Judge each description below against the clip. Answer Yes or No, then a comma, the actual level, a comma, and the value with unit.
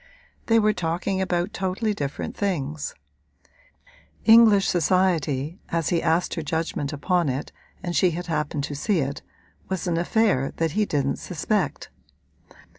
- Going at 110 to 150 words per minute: Yes, average, 140 wpm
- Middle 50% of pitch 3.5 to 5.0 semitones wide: Yes, average, 4.2 semitones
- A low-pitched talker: No, medium, 175 Hz